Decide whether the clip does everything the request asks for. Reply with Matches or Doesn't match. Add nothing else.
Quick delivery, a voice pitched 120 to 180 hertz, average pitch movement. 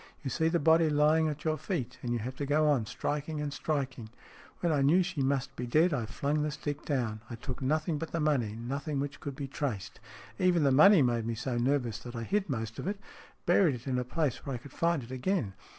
Matches